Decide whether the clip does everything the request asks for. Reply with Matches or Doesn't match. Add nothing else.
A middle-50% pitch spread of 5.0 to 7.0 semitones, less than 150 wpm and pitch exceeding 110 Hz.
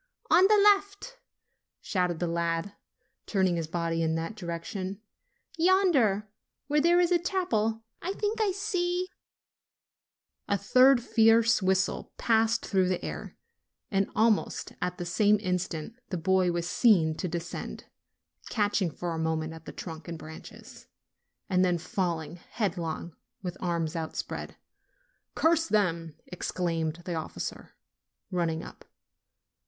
Matches